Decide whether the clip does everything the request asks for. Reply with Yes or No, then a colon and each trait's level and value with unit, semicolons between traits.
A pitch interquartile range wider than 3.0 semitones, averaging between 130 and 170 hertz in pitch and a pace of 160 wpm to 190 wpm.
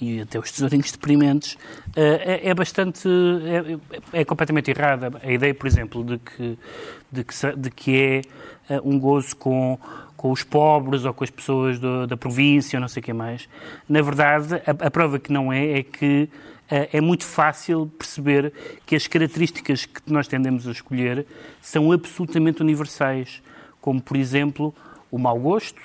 No: average, 2.7 semitones; medium, 140 Hz; average, 165 wpm